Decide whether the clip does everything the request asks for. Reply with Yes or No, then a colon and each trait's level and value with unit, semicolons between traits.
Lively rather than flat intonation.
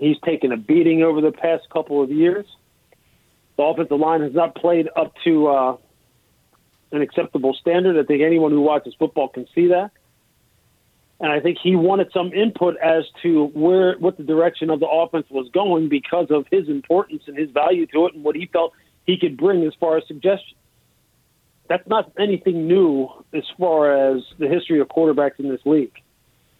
No: average, 2.9 semitones